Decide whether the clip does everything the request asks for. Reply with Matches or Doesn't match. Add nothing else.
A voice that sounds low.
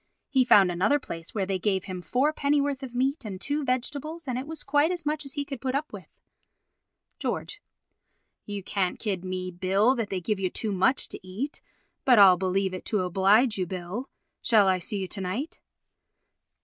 Doesn't match